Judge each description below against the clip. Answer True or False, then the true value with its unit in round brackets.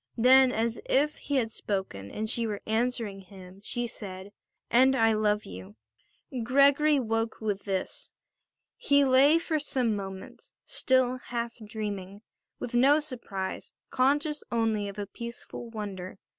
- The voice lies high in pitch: True (225 Hz)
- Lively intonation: False (4.3 semitones)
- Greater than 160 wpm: False (140 wpm)